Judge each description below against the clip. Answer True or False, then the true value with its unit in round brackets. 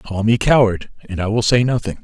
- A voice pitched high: False (110 Hz)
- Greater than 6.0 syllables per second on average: False (5.6 syllables/s)